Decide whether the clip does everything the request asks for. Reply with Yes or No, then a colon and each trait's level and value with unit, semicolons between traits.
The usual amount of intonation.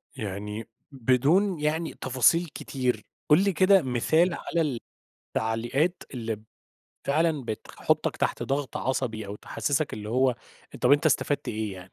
No: wide, 5.8 semitones